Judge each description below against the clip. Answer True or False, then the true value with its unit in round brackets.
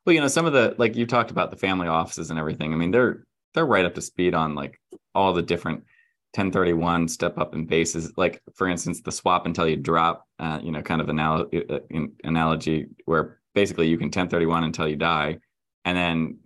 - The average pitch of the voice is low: True (85 Hz)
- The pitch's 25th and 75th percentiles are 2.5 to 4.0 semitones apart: False (2.1 semitones)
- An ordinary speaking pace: False (225 wpm)